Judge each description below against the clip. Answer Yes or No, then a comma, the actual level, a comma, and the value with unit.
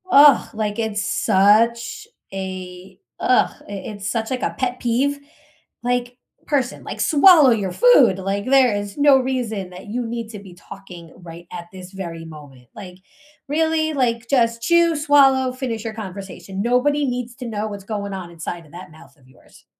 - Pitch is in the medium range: No, high, 220 Hz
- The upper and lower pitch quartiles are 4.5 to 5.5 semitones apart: Yes, average, 5.2 semitones